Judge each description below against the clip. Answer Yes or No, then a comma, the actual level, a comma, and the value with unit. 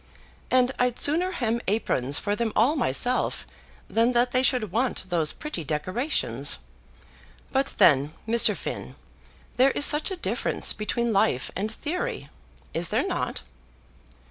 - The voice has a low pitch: No, high, 235 Hz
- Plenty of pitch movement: Yes, wide, 5.8 semitones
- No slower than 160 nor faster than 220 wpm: No, average, 140 wpm